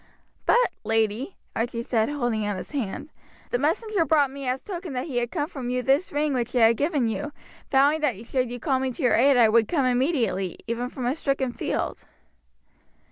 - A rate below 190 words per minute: No, fast, 205 wpm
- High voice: Yes, very high, 260 Hz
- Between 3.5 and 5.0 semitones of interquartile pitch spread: Yes, average, 3.8 semitones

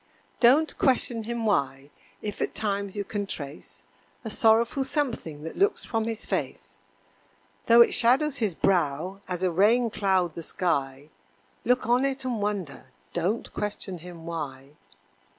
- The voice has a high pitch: Yes, high, 205 Hz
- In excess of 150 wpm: No, average, 145 wpm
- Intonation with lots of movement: Yes, wide, 5.9 semitones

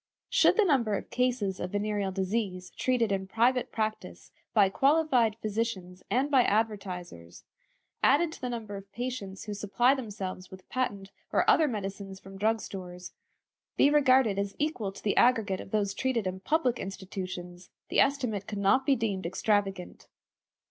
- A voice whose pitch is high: Yes, high, 210 Hz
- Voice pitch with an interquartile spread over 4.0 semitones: Yes, average, 4.5 semitones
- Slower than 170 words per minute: Yes, average, 160 wpm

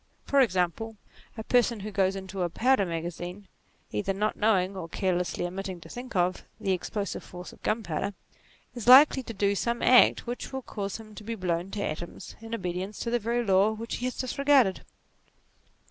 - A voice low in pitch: No, high, 200 Hz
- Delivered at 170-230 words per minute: Yes, average, 190 wpm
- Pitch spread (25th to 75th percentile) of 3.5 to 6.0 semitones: Yes, average, 4.1 semitones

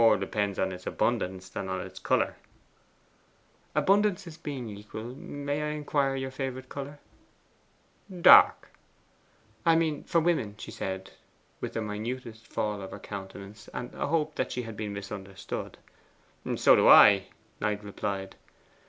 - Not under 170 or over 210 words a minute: No, average, 140 wpm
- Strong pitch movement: Yes, wide, 6.2 semitones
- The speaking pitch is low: Yes, low, 115 Hz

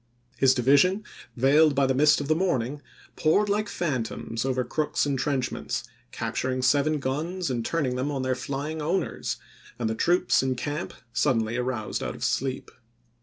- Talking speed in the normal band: Yes, average, 165 wpm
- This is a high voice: No, low, 135 Hz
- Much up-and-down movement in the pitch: No, average, 3.3 semitones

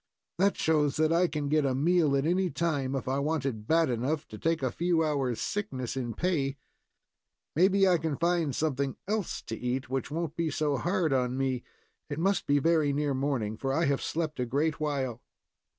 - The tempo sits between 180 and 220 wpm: Yes, average, 200 wpm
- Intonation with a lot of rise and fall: No, average, 3.8 semitones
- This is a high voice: No, medium, 145 Hz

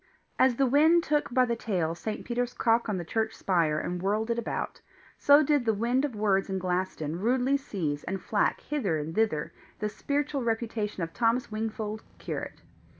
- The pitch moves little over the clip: No, average, 4.8 semitones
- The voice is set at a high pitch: Yes, high, 220 Hz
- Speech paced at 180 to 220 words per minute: Yes, average, 185 wpm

